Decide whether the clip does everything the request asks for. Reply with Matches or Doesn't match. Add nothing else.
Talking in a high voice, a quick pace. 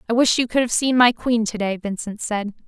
Matches